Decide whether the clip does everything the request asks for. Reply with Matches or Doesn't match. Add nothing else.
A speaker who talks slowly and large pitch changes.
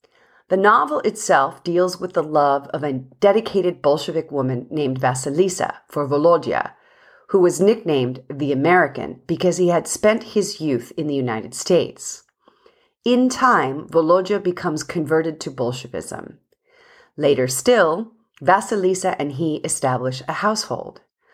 Matches